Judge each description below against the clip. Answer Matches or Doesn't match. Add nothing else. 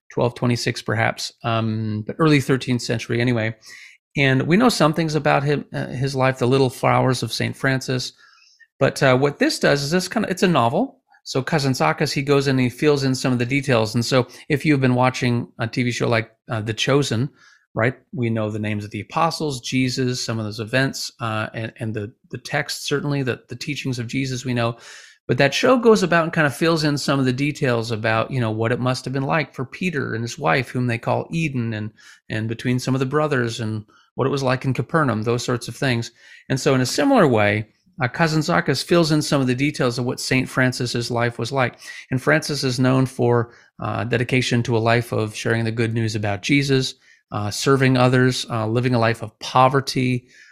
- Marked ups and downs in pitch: Doesn't match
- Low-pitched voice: Matches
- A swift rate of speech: Matches